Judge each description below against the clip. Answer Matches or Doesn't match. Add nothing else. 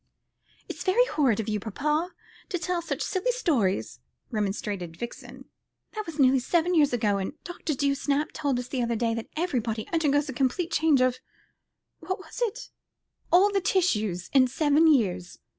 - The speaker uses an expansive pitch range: Matches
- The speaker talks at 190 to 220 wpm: Doesn't match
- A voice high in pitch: Matches